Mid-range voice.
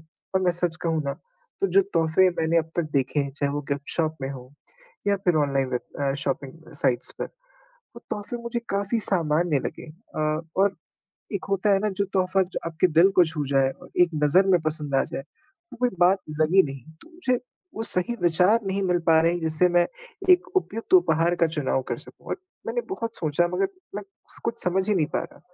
Yes: medium, 175 Hz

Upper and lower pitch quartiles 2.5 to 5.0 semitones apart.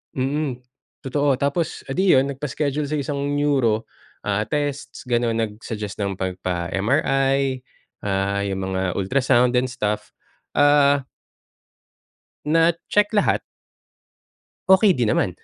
No: wide, 5.5 semitones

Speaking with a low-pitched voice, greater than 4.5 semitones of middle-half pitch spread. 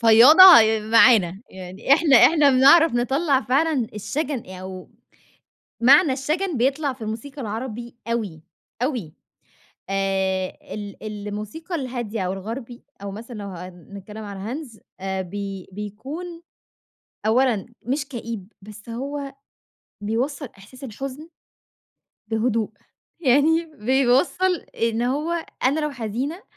No: high, 235 Hz; average, 5.0 semitones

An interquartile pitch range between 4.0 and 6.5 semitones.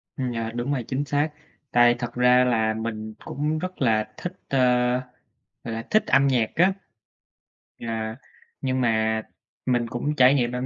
No: average, 3.3 semitones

